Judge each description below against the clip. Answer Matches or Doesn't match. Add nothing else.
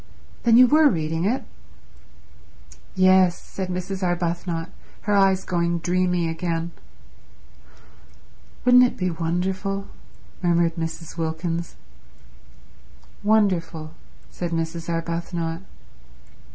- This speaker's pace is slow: Matches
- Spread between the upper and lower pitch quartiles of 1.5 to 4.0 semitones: Matches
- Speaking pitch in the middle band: Matches